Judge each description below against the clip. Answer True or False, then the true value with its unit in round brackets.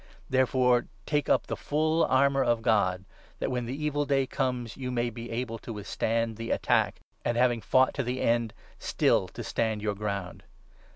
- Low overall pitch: True (120 Hz)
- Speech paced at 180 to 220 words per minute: True (185 wpm)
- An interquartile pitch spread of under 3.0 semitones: True (2.5 semitones)